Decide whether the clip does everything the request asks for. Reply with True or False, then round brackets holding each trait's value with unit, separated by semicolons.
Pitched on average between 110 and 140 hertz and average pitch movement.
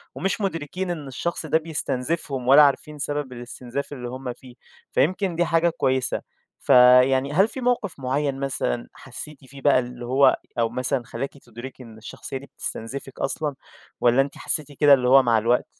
True (135 Hz; 3.2 semitones)